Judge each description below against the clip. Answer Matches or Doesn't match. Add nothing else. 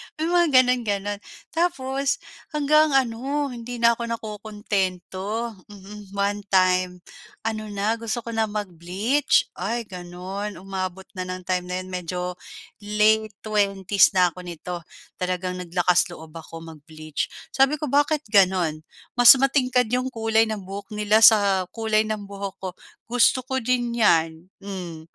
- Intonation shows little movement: Doesn't match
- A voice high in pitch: Matches